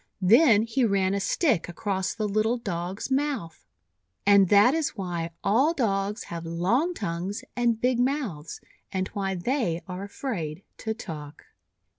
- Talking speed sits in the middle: Yes, average, 145 wpm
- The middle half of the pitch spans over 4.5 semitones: Yes, average, 5.3 semitones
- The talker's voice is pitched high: Yes, high, 200 Hz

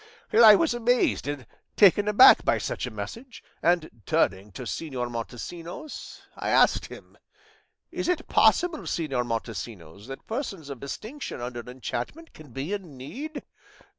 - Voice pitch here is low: No, medium, 160 Hz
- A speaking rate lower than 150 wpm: Yes, average, 140 wpm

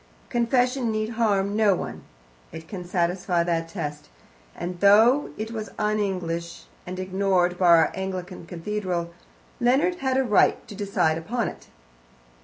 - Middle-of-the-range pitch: No, high, 195 Hz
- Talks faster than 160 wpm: No, average, 145 wpm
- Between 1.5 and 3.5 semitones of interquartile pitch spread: No, average, 4.0 semitones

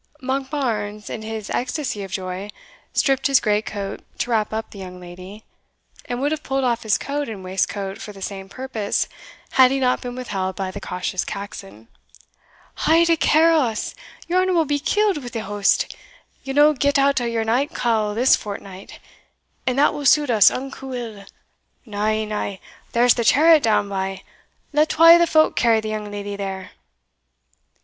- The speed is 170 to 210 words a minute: Yes, average, 180 wpm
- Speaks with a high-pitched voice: Yes, high, 225 Hz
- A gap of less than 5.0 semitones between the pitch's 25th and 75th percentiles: No, average, 5.3 semitones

